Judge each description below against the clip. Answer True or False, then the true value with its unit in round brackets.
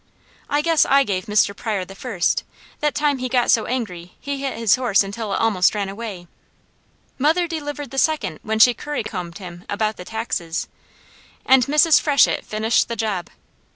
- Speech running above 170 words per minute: True (180 wpm)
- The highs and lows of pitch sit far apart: True (5.9 semitones)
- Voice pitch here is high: True (225 Hz)